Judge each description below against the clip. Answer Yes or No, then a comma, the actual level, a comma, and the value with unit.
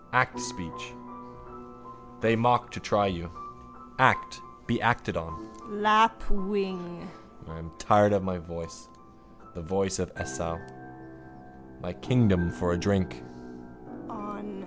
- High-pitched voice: No, low, 100 Hz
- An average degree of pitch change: No, wide, 6.3 semitones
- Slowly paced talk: Yes, slow, 110 wpm